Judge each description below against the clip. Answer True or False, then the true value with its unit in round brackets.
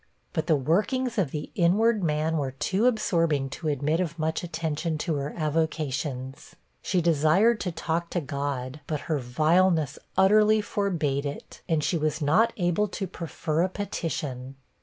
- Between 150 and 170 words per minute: True (160 wpm)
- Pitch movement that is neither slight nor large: True (3.8 semitones)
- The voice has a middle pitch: True (160 Hz)